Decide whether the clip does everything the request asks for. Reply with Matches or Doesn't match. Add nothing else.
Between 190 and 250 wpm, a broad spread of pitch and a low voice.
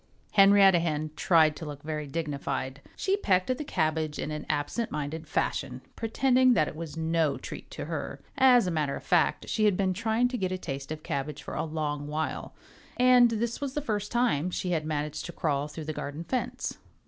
Doesn't match